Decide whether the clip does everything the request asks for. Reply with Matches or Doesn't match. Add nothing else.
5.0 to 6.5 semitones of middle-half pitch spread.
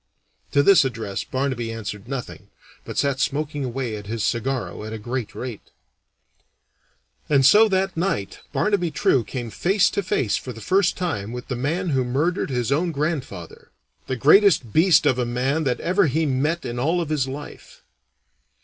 Matches